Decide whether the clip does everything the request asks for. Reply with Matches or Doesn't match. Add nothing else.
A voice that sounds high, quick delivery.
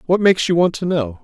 Doesn't match